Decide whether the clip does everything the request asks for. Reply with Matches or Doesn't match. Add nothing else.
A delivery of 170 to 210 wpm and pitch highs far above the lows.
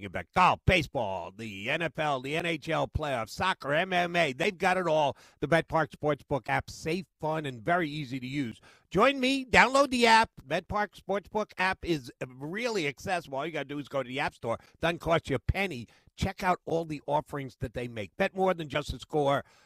Doesn't match